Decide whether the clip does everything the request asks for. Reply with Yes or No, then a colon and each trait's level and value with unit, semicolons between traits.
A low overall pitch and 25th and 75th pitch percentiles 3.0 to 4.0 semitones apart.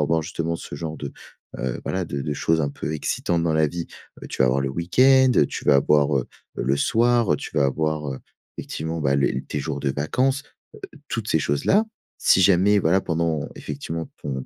Yes: very low, 80 Hz; average, 3.7 semitones